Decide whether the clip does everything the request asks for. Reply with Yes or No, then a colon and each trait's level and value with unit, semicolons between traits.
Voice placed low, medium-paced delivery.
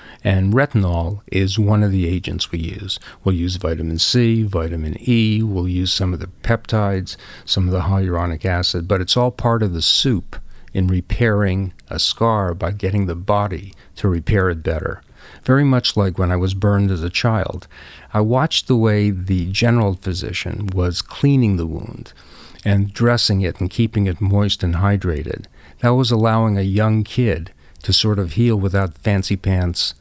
Yes: very low, 95 Hz; average, 175 wpm